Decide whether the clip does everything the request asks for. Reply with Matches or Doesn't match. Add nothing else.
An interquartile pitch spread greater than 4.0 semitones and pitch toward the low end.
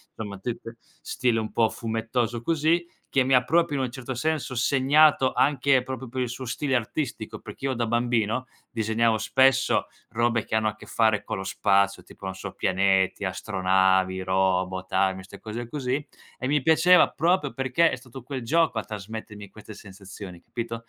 Matches